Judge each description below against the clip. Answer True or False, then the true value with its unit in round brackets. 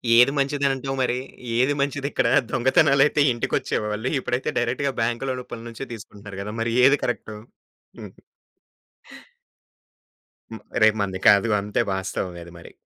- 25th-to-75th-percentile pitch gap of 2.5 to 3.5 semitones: False (4.4 semitones)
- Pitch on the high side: False (120 Hz)